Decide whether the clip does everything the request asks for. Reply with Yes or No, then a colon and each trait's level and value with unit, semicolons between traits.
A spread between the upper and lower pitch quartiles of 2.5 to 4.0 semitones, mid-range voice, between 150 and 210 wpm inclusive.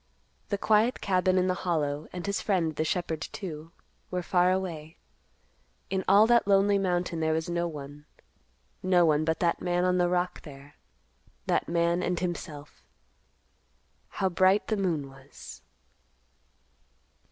No: average, 2.9 semitones; medium, 175 Hz; average, 140 wpm